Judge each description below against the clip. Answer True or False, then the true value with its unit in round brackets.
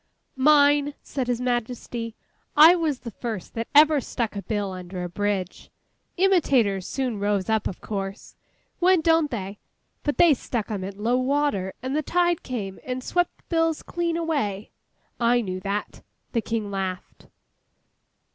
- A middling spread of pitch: False (6.5 semitones)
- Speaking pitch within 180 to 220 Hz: False (240 Hz)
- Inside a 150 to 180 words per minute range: True (155 wpm)